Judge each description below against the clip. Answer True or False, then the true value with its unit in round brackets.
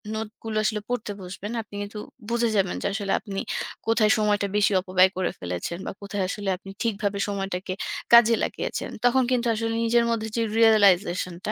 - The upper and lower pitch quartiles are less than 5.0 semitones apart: True (2.6 semitones)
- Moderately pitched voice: False (205 Hz)